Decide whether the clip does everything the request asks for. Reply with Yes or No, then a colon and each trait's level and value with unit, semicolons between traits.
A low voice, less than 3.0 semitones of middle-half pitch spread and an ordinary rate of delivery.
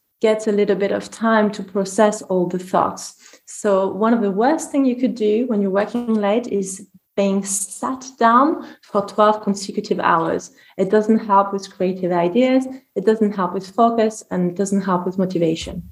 No: high, 205 Hz; narrow, 2.5 semitones; average, 185 wpm